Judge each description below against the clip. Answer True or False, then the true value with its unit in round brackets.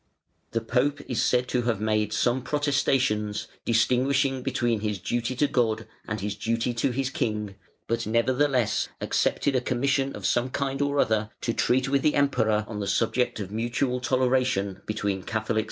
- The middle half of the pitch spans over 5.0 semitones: False (3.5 semitones)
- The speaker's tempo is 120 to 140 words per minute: False (175 wpm)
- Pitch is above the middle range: False (120 Hz)